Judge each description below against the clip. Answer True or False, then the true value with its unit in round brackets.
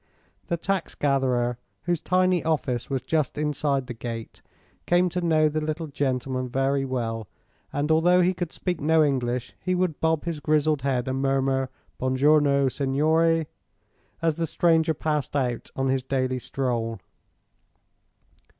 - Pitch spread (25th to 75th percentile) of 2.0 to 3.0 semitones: False (3.7 semitones)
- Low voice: False (145 Hz)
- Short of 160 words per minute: True (150 wpm)